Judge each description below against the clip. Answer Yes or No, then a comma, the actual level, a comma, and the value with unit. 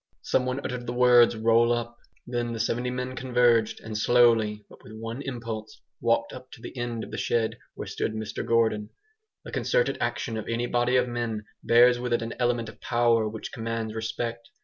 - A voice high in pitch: No, low, 115 Hz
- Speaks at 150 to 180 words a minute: No, average, 195 wpm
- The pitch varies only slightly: Yes, narrow, 1.4 semitones